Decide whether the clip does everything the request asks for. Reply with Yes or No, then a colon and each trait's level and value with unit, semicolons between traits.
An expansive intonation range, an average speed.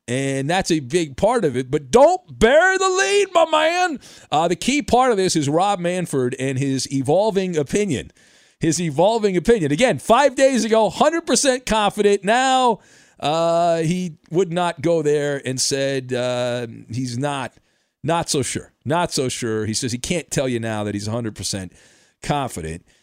Yes: wide, 8.3 semitones; average, 170 wpm